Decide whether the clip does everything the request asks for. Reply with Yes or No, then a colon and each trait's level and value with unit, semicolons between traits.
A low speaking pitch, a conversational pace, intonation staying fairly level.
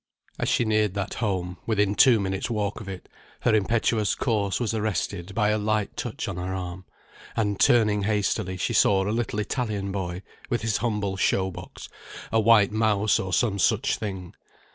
Yes: low, 105 Hz; average, 180 wpm; narrow, 2.2 semitones